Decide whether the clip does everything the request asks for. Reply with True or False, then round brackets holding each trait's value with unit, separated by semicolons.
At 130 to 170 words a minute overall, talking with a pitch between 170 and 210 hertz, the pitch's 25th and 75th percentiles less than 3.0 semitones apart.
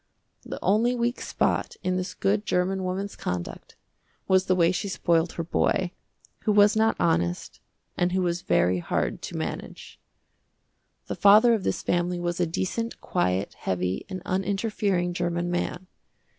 True (155 wpm; 185 Hz; 2.6 semitones)